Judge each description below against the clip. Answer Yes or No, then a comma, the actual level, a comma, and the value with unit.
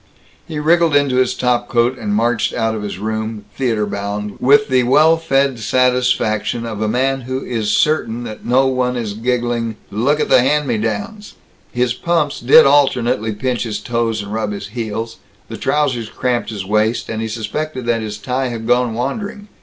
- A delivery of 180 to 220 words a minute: Yes, average, 185 wpm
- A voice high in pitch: No, low, 120 Hz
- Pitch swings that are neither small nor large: Yes, average, 3.1 semitones